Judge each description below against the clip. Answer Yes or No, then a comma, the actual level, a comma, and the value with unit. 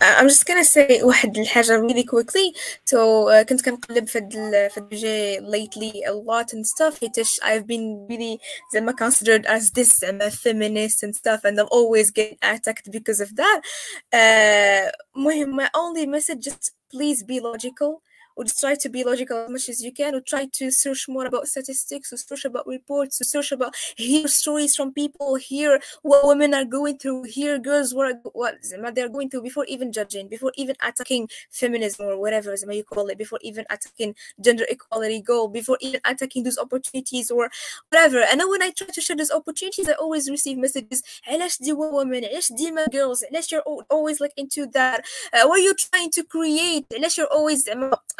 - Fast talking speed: Yes, fast, 180 wpm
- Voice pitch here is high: Yes, very high, 260 Hz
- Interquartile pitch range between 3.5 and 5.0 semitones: Yes, average, 4.4 semitones